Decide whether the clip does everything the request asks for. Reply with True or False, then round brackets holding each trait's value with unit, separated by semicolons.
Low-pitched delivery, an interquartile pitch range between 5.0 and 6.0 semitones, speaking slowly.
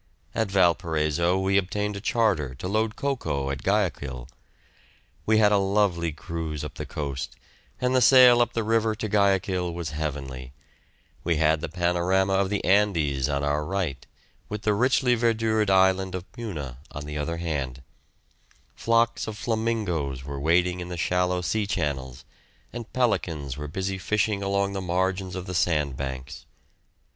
False (90 Hz; 5.6 semitones; 155 wpm)